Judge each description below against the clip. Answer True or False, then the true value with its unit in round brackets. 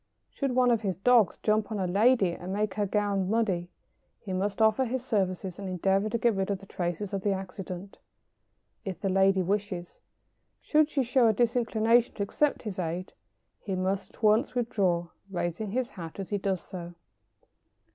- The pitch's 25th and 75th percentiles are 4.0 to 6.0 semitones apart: False (3.3 semitones)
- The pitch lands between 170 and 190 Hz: False (200 Hz)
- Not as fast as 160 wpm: False (185 wpm)